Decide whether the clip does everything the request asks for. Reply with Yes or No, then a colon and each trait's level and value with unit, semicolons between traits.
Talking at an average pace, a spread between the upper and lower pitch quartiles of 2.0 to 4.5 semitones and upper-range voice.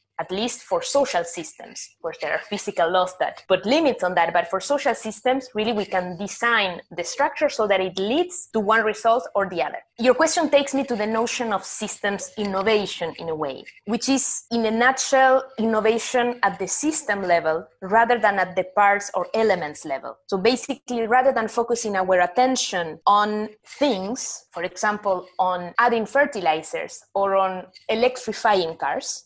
No: average, 170 wpm; average, 5.1 semitones; high, 215 Hz